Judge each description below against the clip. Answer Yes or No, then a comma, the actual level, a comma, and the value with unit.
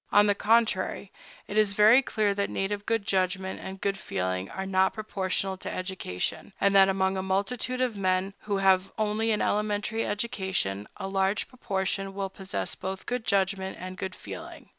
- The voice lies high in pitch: Yes, high, 195 Hz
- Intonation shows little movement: Yes, narrow, 1.7 semitones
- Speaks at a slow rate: No, average, 175 wpm